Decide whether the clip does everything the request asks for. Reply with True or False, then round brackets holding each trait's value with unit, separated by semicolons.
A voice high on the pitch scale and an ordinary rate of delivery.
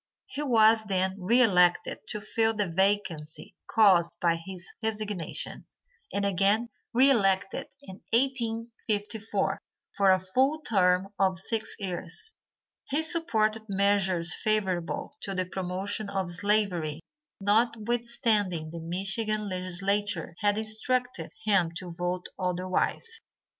False (200 Hz; 115 wpm)